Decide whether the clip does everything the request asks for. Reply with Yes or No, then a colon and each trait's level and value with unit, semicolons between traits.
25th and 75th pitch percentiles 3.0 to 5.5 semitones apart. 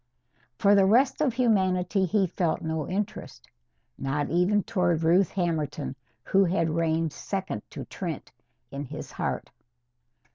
Yes: average, 3.6 semitones